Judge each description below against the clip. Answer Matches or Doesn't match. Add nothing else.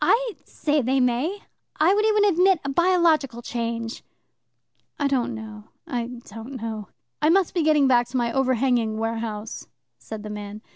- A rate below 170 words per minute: Matches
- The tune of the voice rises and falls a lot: Matches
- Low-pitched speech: Doesn't match